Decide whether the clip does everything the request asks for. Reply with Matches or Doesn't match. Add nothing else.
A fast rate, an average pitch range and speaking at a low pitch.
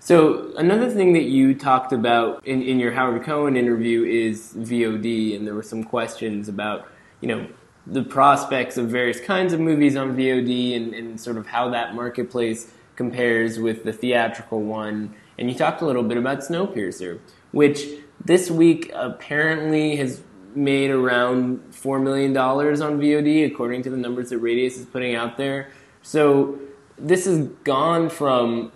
Doesn't match